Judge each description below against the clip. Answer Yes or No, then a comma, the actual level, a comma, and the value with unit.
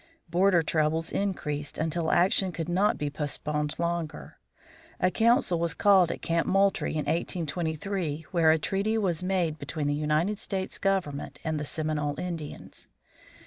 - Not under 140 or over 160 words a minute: Yes, average, 145 wpm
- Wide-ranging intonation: No, average, 3.7 semitones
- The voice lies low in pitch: No, medium, 165 Hz